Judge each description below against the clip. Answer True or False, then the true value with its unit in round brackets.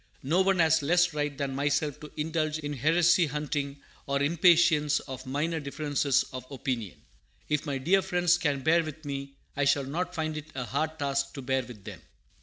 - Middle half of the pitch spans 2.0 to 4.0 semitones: True (2.6 semitones)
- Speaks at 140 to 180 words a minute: False (190 wpm)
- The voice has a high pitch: False (150 Hz)